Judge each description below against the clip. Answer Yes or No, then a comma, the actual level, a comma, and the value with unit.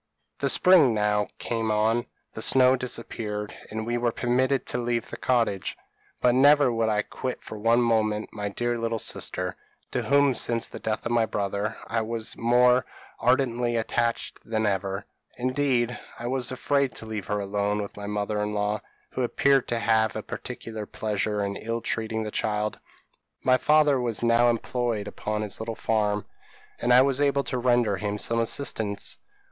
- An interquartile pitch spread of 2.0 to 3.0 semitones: Yes, average, 2.7 semitones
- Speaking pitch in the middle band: No, low, 115 Hz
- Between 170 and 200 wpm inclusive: Yes, average, 175 wpm